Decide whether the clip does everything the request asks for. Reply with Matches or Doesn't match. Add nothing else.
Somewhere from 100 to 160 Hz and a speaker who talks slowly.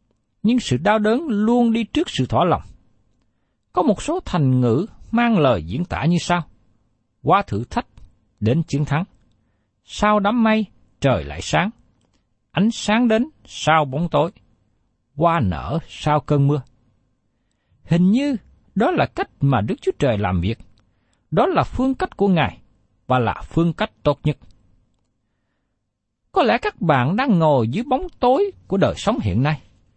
Matches